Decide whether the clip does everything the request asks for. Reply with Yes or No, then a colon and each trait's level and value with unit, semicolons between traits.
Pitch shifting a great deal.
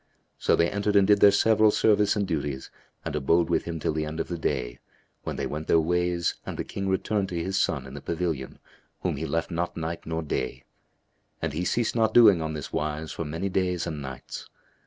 No: average, 4.0 semitones